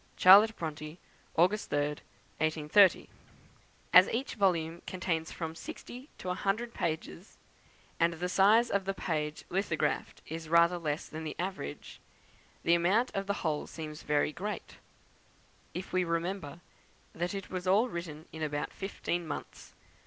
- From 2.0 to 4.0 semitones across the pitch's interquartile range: Yes, average, 3.5 semitones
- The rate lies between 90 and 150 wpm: Yes, average, 145 wpm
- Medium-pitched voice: Yes, medium, 175 Hz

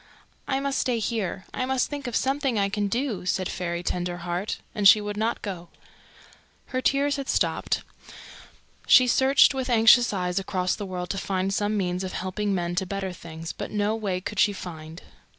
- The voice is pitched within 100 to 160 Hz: No, high, 200 Hz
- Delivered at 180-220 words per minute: Yes, average, 185 wpm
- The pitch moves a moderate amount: Yes, average, 4.8 semitones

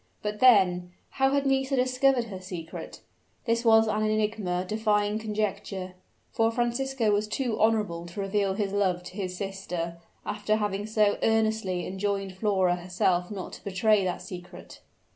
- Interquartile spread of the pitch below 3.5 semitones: Yes, average, 3.0 semitones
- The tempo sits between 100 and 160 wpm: Yes, average, 150 wpm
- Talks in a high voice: Yes, high, 205 Hz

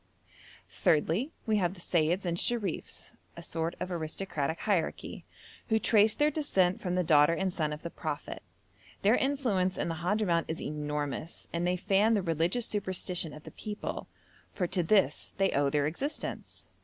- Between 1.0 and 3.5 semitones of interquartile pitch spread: No, average, 4.2 semitones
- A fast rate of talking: No, average, 165 wpm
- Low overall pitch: No, medium, 180 Hz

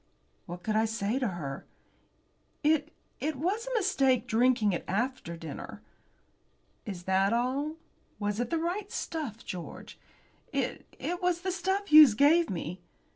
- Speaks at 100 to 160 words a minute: Yes, average, 145 wpm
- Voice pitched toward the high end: Yes, very high, 255 Hz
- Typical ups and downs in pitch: No, wide, 8.6 semitones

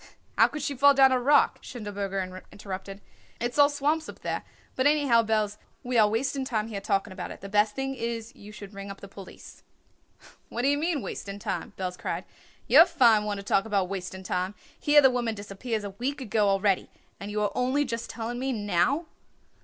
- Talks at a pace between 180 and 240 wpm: Yes, fast, 205 wpm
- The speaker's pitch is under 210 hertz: No, high, 220 Hz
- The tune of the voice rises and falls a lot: No, average, 5.0 semitones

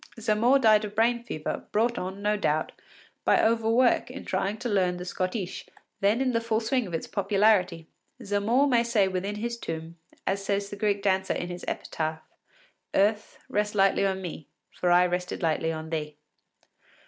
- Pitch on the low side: No, high, 200 Hz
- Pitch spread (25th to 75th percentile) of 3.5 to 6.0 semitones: Yes, average, 3.8 semitones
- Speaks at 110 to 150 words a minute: No, average, 175 wpm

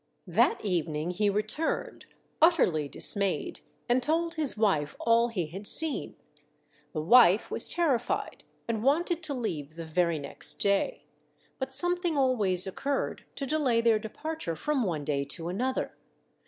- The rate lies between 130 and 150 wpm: Yes, average, 140 wpm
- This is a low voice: No, high, 230 Hz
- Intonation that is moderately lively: No, wide, 8.5 semitones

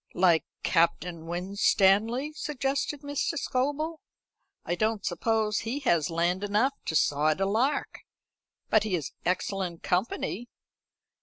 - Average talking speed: No, slow, 120 wpm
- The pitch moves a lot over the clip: Yes, wide, 6.5 semitones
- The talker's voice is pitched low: No, high, 200 Hz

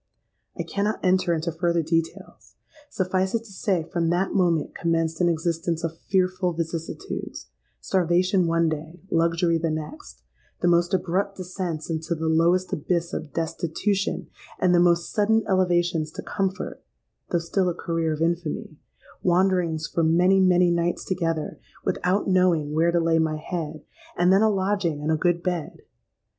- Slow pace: No, average, 150 wpm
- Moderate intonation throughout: No, narrow, 2.1 semitones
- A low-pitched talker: No, medium, 170 Hz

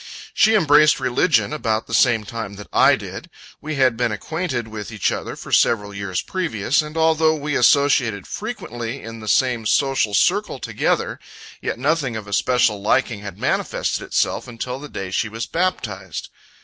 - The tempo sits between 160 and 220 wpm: Yes, average, 170 wpm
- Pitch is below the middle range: Yes, low, 120 Hz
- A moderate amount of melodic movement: No, wide, 5.7 semitones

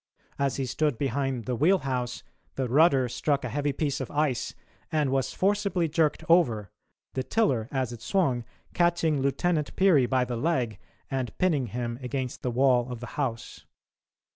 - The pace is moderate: Yes, average, 165 wpm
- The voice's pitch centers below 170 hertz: Yes, low, 135 Hz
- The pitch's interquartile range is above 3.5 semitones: Yes, average, 4.0 semitones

